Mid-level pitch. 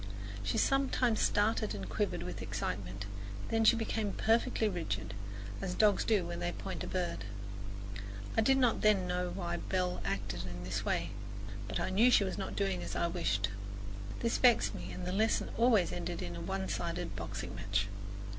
Yes: medium, 180 Hz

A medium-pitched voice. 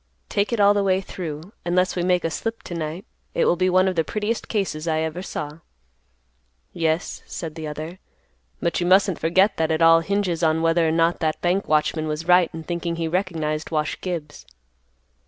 Yes: medium, 170 Hz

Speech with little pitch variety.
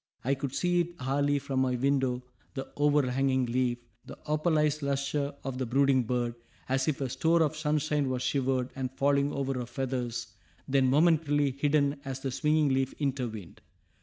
Yes: narrow, 2.2 semitones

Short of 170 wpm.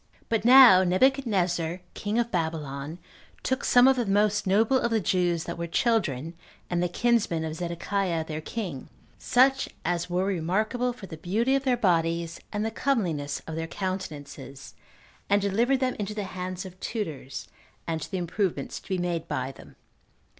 No: average, 175 wpm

